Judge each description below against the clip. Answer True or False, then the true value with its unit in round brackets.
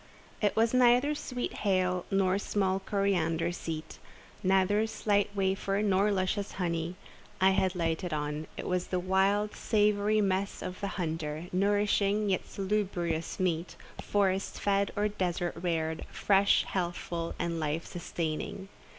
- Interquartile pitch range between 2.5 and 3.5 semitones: True (2.9 semitones)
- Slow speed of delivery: True (130 wpm)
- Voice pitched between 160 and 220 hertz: True (190 Hz)